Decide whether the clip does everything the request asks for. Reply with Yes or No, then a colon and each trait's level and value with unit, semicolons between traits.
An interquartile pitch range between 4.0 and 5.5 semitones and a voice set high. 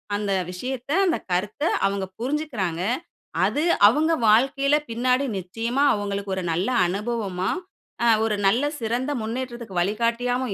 Yes: average, 4.5 semitones; high, 230 Hz